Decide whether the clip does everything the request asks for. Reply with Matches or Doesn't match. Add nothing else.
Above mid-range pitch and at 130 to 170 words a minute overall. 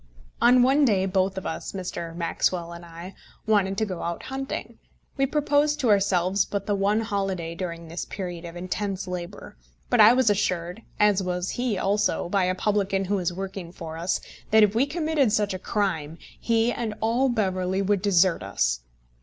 Doesn't match